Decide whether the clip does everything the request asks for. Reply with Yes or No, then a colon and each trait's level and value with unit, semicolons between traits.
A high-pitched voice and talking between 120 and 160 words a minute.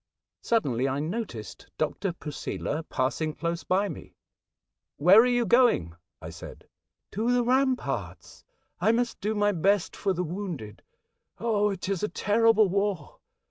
Yes: high, 200 Hz; average, 155 wpm